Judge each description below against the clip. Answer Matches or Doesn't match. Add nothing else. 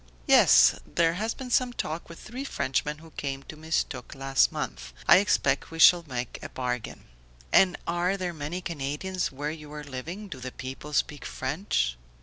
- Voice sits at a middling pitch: Matches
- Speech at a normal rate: Matches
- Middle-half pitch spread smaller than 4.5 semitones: Doesn't match